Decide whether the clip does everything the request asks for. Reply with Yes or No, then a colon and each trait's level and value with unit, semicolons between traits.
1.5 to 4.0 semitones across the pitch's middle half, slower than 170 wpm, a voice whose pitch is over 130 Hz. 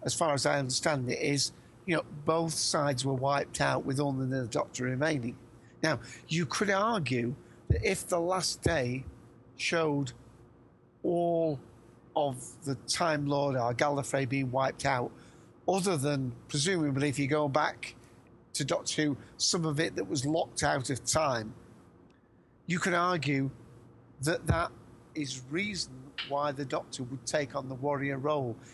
Yes: average, 3.7 semitones; average, 155 wpm; medium, 140 Hz